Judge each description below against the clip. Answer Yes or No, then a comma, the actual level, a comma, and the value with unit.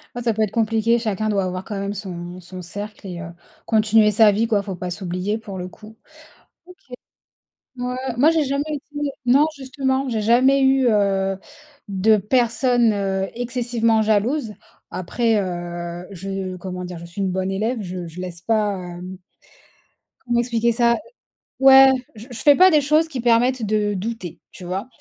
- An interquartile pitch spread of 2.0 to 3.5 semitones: No, average, 4.2 semitones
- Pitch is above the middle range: Yes, high, 215 Hz